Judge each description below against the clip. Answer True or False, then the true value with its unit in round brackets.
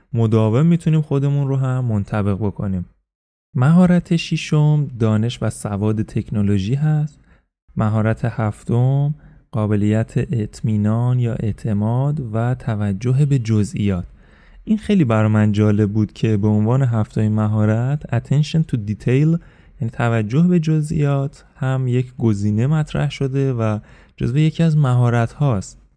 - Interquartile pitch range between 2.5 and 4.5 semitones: False (5.1 semitones)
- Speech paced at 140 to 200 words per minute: False (125 wpm)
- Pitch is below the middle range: True (120 Hz)